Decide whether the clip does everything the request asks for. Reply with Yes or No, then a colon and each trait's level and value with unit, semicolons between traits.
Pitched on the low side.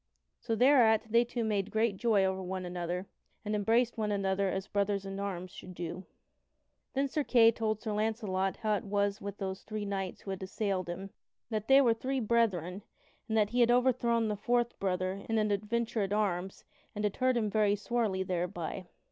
No: high, 205 Hz